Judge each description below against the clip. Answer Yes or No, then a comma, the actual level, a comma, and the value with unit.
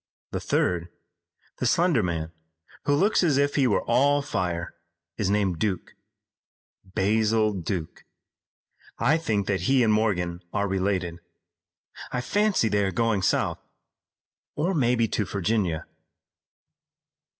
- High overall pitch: No, low, 105 Hz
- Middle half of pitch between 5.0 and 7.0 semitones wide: Yes, wide, 5.6 semitones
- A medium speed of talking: No, slow, 125 wpm